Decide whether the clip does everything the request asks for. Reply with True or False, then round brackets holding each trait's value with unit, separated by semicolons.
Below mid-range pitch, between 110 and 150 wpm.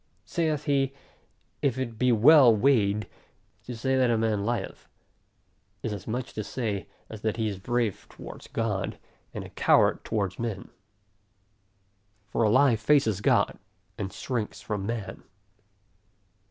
True (115 Hz; 140 wpm)